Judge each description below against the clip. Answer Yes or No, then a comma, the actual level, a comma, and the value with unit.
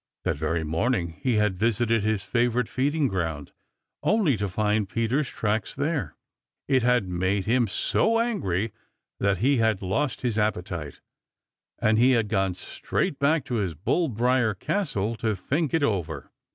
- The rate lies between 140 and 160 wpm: Yes, average, 155 wpm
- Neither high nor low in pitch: No, low, 110 Hz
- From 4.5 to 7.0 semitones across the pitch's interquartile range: Yes, average, 5.1 semitones